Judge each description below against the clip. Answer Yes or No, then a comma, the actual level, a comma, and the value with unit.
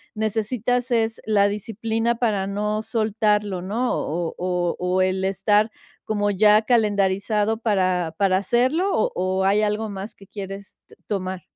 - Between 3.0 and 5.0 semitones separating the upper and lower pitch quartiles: No, narrow, 2.6 semitones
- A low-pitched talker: No, high, 205 Hz